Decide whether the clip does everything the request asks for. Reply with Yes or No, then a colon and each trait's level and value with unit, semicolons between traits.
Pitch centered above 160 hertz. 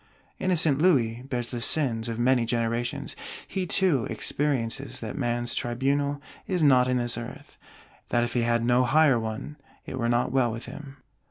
No: low, 125 Hz